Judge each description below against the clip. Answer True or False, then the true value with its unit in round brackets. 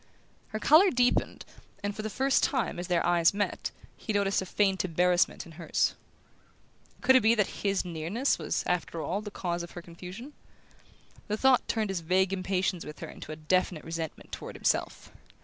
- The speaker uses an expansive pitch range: False (3.8 semitones)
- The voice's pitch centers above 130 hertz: True (190 Hz)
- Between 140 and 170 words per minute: False (185 wpm)